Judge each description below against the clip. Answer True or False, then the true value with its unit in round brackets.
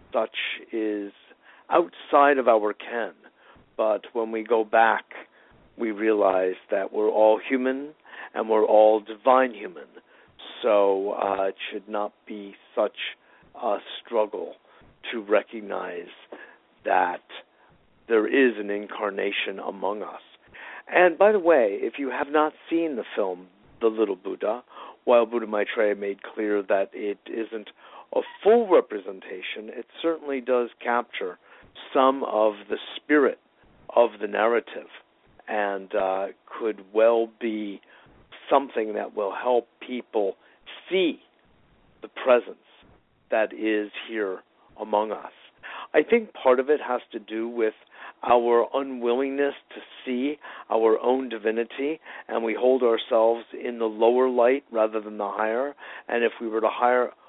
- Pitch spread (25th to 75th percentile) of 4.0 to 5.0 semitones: False (3.6 semitones)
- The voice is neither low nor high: False (115 Hz)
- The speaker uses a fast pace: False (135 wpm)